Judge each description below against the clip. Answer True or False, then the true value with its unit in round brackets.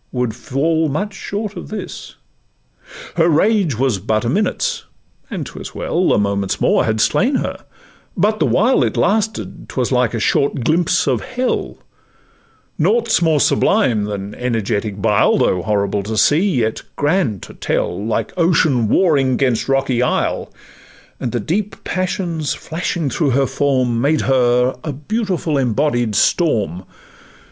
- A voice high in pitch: False (135 Hz)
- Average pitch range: False (7.7 semitones)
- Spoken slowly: False (150 wpm)